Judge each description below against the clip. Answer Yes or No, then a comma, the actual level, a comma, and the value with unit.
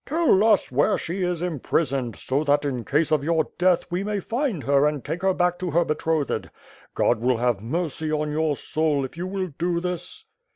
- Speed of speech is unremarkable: No, fast, 210 wpm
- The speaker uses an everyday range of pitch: Yes, average, 4.0 semitones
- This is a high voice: No, medium, 160 Hz